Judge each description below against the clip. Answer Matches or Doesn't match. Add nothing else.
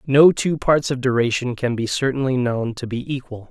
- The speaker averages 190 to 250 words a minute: Matches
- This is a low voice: Matches